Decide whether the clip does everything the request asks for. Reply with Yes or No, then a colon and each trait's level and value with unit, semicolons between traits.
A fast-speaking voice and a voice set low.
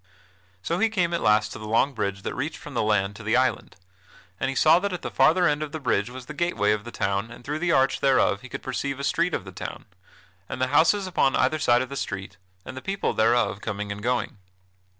Yes: fast, 250 wpm; low, 130 Hz